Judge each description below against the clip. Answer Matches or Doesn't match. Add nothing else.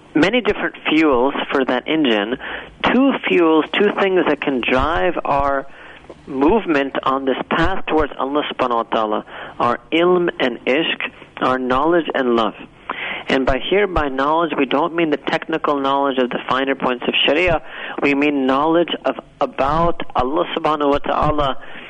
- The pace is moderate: Matches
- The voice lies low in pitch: Doesn't match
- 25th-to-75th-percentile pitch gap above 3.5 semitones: Matches